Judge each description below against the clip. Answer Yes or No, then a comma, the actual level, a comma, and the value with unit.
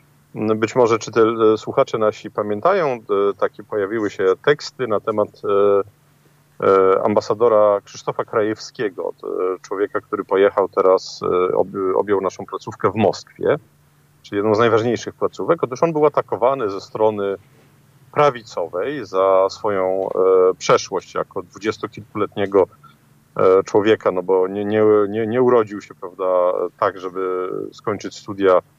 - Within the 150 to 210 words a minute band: No, average, 115 wpm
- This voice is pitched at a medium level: No, low, 115 Hz